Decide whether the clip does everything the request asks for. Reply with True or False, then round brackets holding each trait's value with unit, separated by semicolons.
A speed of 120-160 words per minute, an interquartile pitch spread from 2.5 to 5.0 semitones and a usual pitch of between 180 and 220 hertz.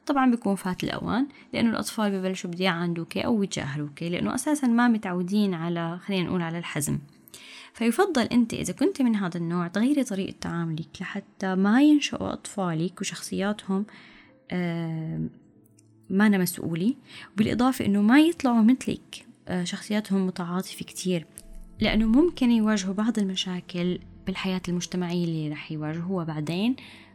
True (130 wpm; 4.5 semitones; 190 Hz)